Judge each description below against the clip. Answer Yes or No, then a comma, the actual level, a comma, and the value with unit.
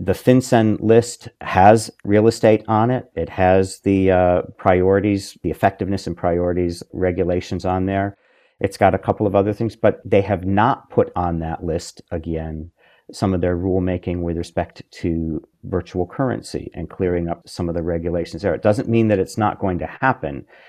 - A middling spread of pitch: Yes, average, 3.1 semitones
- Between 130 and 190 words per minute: Yes, average, 180 wpm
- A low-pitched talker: Yes, very low, 95 Hz